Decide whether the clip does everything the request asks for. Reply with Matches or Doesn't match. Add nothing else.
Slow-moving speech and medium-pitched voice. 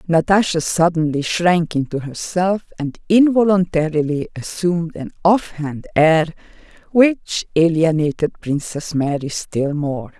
Matches